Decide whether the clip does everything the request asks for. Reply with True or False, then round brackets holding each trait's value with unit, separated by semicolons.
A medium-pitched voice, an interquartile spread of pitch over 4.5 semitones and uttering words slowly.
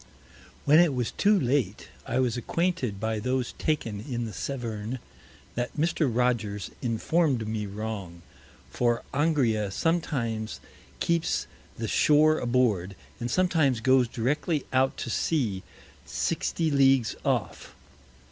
False (125 Hz; 5.0 semitones; 120 wpm)